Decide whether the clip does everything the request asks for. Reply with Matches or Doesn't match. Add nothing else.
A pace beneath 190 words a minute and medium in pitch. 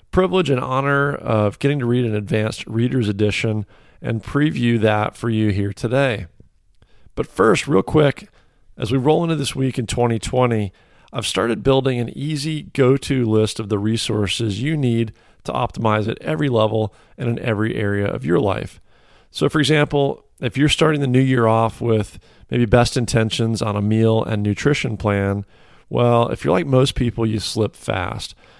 Doesn't match